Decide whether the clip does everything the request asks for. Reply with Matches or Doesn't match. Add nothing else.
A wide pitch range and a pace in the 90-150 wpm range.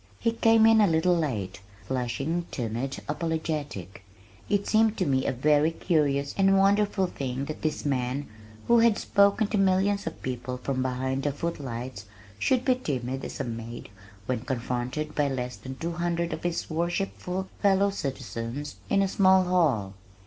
Doesn't match